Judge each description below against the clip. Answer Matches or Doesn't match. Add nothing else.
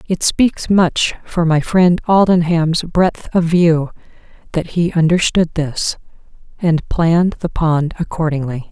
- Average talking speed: Doesn't match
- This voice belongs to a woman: Matches